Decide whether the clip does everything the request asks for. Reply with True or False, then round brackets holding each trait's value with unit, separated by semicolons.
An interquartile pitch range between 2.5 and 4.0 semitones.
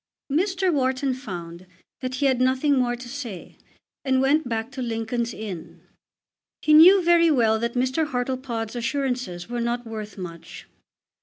True (3.4 semitones)